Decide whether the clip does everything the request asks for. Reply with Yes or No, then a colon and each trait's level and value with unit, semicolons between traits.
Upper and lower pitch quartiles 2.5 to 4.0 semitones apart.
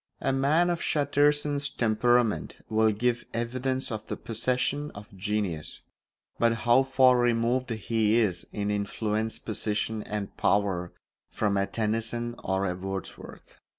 Yes: average, 3.5 semitones